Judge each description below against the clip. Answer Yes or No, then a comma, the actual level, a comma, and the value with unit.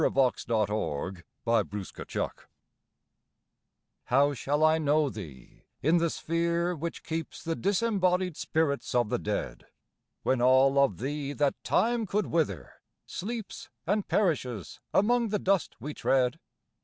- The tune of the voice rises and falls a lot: Yes, wide, 6.1 semitones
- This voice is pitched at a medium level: Yes, medium, 150 Hz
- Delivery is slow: Yes, slow, 130 wpm